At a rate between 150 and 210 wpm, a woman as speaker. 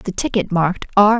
Yes: average, 200 wpm; female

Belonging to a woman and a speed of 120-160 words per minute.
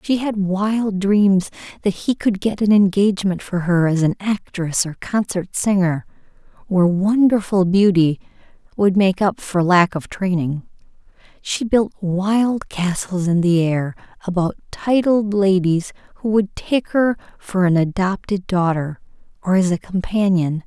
Yes: female; average, 145 wpm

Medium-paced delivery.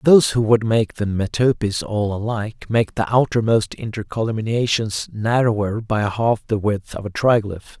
Yes: average, 155 wpm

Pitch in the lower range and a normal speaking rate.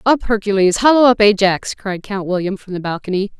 No: high, 205 Hz; average, 195 wpm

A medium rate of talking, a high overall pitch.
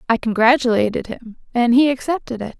Yes: average, 160 wpm; high, 245 Hz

